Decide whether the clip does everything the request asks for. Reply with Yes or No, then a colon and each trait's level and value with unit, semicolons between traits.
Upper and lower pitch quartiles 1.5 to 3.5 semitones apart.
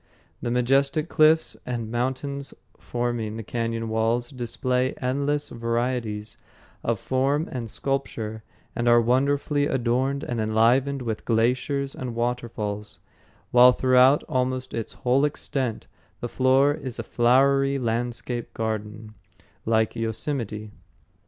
Yes: average, 2.9 semitones